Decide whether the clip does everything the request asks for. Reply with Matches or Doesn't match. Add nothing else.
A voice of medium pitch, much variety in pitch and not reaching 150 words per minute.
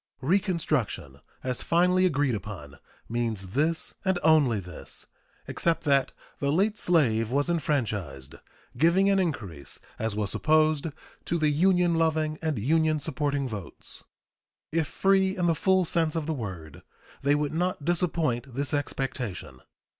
Matches